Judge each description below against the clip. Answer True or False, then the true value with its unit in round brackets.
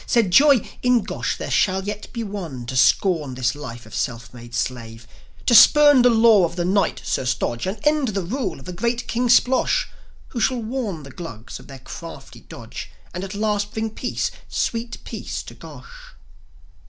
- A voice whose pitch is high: True (195 Hz)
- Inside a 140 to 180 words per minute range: False (190 wpm)